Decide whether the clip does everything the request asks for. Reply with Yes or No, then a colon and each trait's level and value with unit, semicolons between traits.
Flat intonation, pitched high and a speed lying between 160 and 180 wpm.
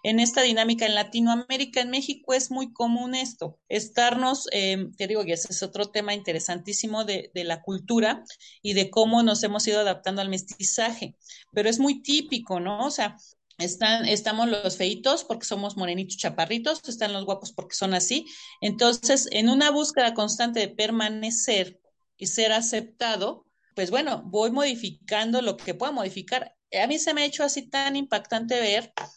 No: average, 3.9 semitones; high, 220 Hz; average, 170 wpm